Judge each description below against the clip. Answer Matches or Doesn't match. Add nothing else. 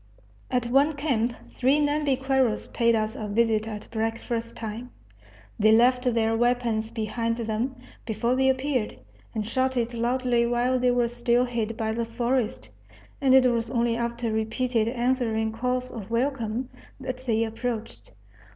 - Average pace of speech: Matches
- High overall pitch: Matches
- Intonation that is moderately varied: Doesn't match